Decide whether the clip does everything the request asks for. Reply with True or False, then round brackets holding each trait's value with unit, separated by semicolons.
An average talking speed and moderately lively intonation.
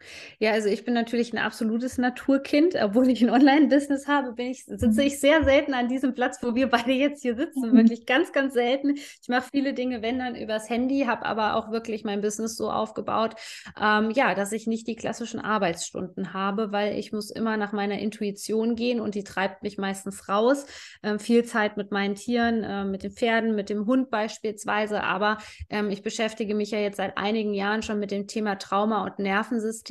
False (205 wpm; 3.2 semitones)